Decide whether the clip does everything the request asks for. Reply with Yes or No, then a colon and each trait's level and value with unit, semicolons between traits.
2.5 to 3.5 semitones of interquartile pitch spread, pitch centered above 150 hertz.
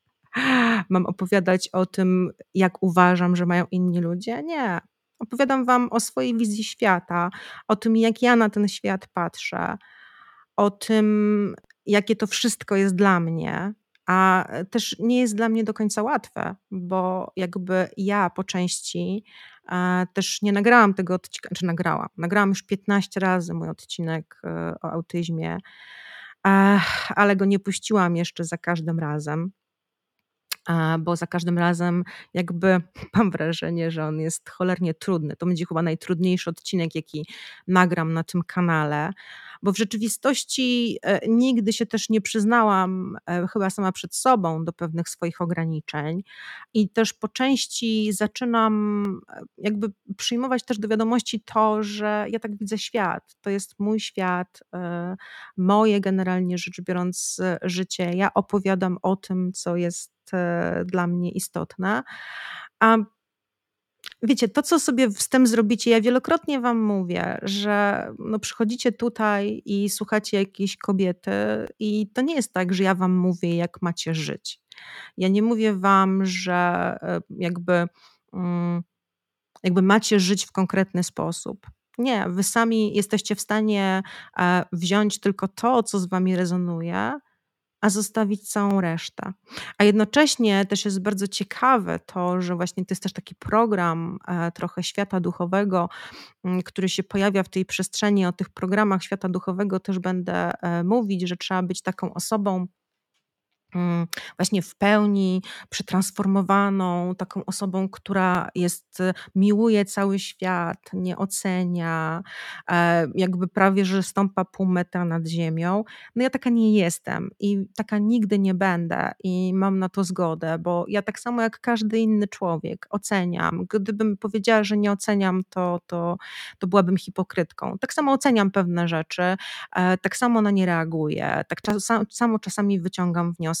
Yes: average, 3.0 semitones; high, 190 Hz